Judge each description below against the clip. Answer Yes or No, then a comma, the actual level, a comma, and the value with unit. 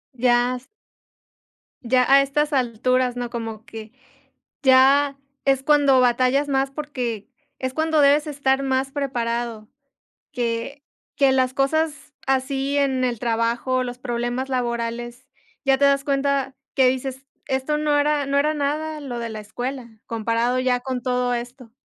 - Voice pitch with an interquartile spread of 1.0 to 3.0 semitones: Yes, narrow, 2.5 semitones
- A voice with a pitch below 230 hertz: No, very high, 260 Hz